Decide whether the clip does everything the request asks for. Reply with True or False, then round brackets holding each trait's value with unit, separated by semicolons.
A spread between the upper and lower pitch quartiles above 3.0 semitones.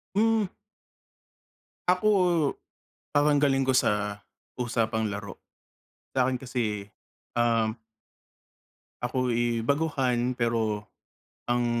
True (4.0 semitones)